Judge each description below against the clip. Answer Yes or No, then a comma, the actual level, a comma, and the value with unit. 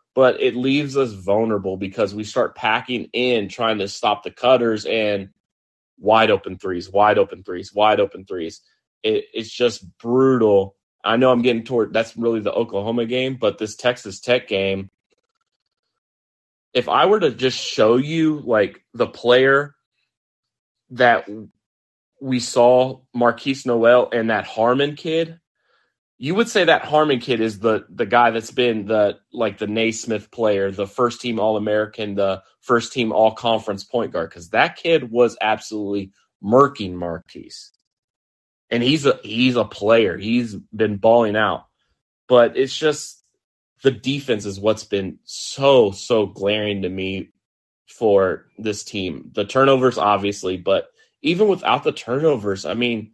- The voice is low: Yes, low, 115 Hz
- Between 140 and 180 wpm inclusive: Yes, average, 150 wpm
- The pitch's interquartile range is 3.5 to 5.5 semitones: Yes, average, 4.0 semitones